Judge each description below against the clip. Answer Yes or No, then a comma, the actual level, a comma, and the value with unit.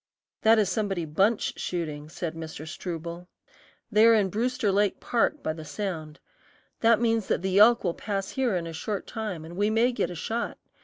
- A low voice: No, high, 195 Hz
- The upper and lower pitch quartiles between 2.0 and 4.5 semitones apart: No, average, 4.9 semitones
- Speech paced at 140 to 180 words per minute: No, average, 195 wpm